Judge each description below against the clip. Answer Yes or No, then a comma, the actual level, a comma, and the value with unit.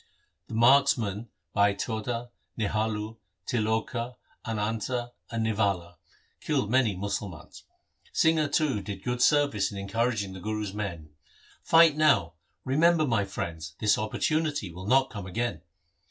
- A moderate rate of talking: No, slow, 130 wpm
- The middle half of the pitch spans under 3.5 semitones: No, average, 3.9 semitones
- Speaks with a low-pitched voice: Yes, low, 110 Hz